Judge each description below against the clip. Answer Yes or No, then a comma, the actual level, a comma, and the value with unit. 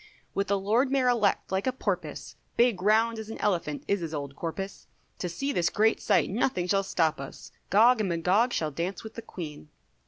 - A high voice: Yes, high, 200 Hz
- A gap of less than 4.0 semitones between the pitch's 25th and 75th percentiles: No, average, 4.8 semitones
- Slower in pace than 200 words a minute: No, fast, 205 wpm